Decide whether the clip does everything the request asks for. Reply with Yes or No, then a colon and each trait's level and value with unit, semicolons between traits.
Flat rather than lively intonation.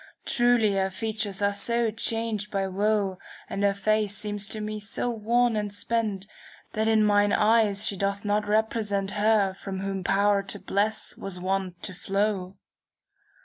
Yes: narrow, 1.7 semitones